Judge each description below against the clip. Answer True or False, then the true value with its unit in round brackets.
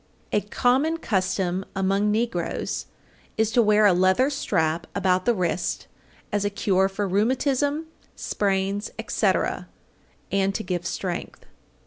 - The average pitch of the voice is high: True (200 Hz)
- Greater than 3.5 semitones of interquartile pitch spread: False (3.0 semitones)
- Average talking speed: False (125 wpm)